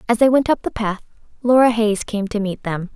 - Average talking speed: No, fast, 245 wpm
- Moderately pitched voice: No, high, 220 Hz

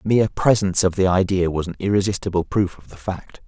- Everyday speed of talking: No, fast, 225 wpm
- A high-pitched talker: No, very low, 95 Hz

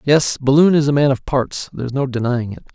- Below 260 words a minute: No, fast, 265 wpm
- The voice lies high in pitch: No, low, 135 Hz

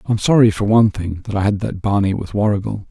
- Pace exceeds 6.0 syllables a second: Yes, 6.2 syllables/s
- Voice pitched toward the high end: No, low, 105 Hz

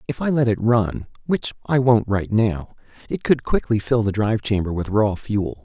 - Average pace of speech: Yes, average, 190 wpm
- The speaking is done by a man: Yes, male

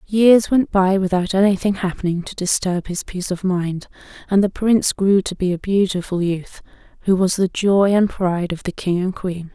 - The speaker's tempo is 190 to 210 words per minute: Yes, average, 200 wpm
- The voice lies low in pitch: No, high, 190 Hz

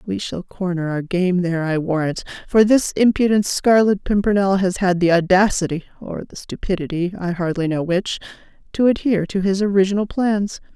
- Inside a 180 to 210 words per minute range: No, average, 155 wpm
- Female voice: Yes, female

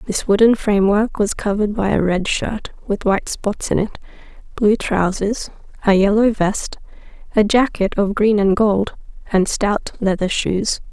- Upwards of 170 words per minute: No, average, 150 wpm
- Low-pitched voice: No, high, 205 Hz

